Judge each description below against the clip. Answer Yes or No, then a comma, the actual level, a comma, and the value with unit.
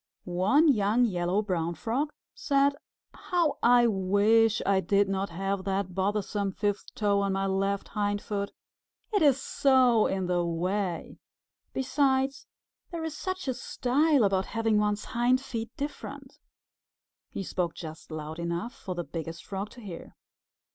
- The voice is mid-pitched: No, high, 205 Hz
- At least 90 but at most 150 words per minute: Yes, average, 145 wpm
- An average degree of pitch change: Yes, average, 4.9 semitones